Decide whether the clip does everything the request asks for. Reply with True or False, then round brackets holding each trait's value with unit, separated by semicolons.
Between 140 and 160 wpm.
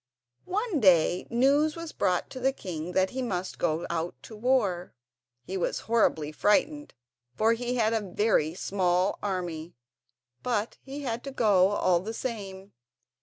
True (155 wpm)